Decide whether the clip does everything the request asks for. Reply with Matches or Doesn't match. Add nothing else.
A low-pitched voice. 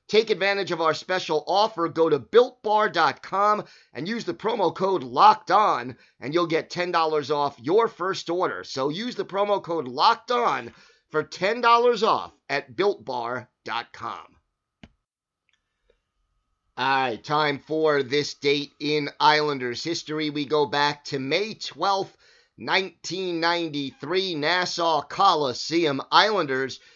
Doesn't match